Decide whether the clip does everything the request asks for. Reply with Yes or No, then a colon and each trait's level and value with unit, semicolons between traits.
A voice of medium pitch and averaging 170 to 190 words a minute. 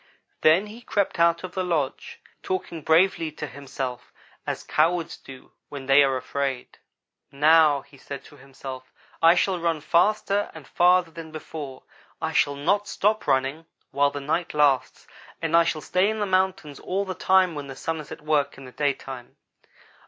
Yes: medium, 155 Hz; average, 175 wpm